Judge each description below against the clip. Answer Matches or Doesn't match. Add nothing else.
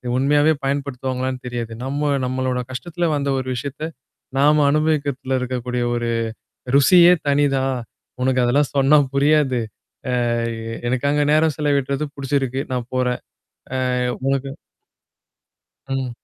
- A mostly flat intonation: Matches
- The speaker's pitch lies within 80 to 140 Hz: Matches